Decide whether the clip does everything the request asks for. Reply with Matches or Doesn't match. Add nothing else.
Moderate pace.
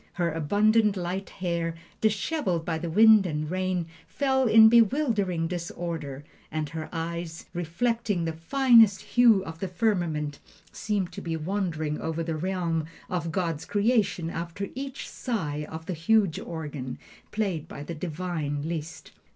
Matches